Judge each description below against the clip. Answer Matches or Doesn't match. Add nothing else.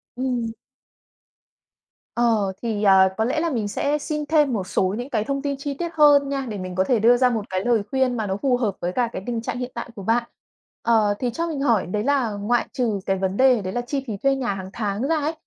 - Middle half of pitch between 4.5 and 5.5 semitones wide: Matches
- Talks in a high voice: Matches